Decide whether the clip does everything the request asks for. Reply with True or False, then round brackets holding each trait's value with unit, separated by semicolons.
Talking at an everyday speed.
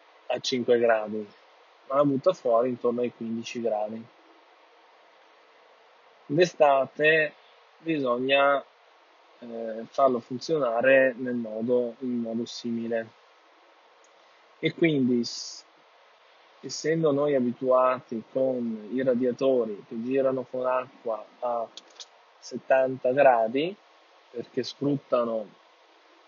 False (85 wpm)